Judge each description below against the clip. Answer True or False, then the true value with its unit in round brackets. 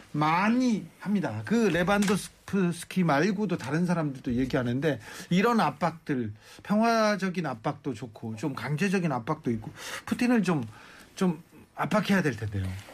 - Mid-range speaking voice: True (165 Hz)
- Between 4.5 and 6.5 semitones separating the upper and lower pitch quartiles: False (7.0 semitones)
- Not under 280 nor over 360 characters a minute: True (300 characters per minute)